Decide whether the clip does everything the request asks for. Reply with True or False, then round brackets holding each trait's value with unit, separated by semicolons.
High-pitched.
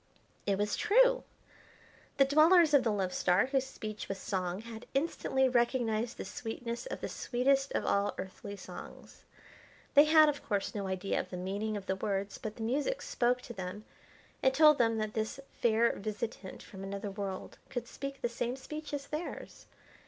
True (230 Hz)